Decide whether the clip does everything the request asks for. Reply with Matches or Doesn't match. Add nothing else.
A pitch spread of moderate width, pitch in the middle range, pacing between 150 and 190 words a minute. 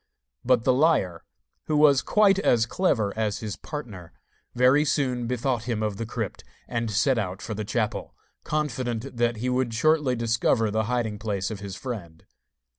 Doesn't match